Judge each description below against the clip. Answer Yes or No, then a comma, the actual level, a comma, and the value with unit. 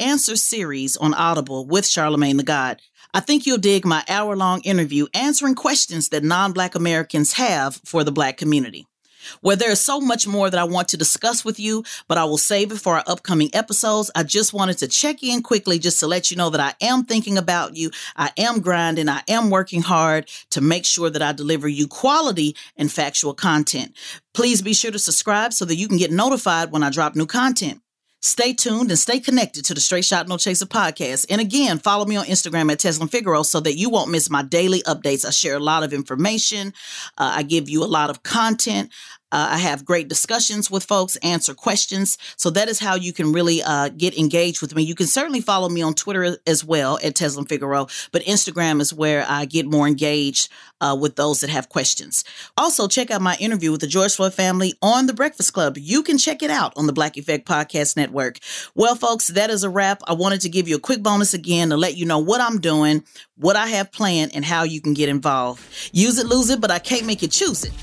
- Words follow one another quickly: Yes, fast, 230 wpm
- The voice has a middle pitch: Yes, medium, 175 Hz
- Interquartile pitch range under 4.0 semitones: No, wide, 5.5 semitones